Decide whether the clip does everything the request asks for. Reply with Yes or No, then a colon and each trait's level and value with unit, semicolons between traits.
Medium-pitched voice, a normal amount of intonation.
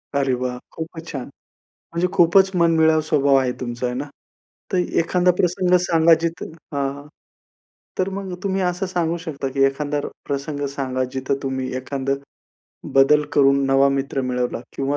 Yes: medium, 145 Hz; average, 3.7 semitones